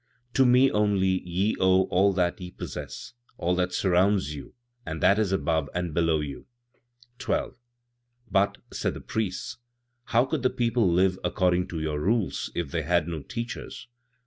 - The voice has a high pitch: No, very low, 95 Hz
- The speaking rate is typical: Yes, average, 165 wpm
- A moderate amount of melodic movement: Yes, average, 3.6 semitones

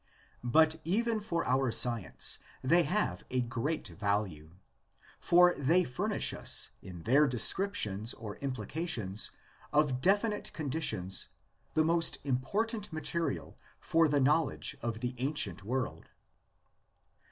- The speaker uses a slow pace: Yes, slow, 115 wpm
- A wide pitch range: Yes, wide, 6.8 semitones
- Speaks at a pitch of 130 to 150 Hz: Yes, medium, 140 Hz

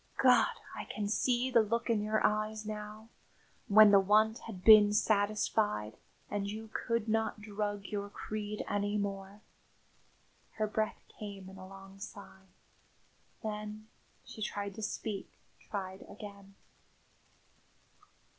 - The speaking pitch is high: Yes, high, 210 Hz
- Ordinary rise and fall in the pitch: No, narrow, 1.3 semitones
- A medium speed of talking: No, slow, 125 wpm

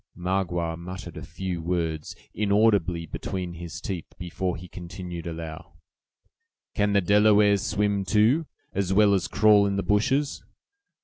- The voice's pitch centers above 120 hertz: No, very low, 95 Hz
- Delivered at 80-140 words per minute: Yes, slow, 135 wpm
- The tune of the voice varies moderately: Yes, average, 3.1 semitones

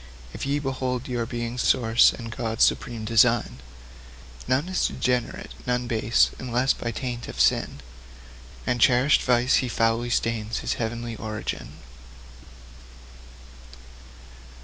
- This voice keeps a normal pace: No, slow, 120 wpm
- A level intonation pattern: Yes, narrow, 1.6 semitones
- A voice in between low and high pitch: No, low, 120 Hz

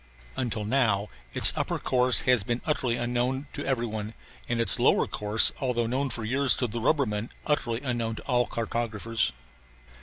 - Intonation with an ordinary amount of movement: No, narrow, 2.3 semitones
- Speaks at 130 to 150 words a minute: No, average, 170 wpm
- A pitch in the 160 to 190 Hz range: No, low, 120 Hz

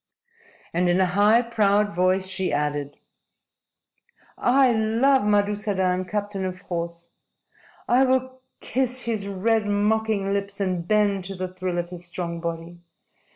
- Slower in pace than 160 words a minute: Yes, slow, 135 wpm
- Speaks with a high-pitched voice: Yes, high, 200 Hz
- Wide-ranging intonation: No, average, 3.3 semitones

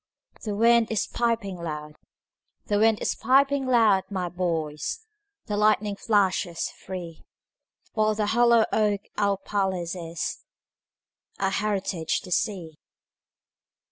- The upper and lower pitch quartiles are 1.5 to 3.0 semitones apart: No, average, 3.9 semitones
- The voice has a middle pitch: No, high, 205 Hz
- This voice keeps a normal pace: No, slow, 100 wpm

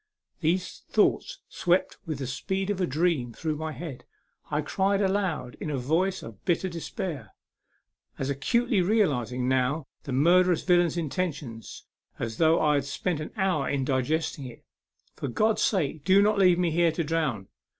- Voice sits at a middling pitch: Yes, medium, 160 Hz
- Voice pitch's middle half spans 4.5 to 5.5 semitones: Yes, average, 5.1 semitones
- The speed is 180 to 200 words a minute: No, average, 170 wpm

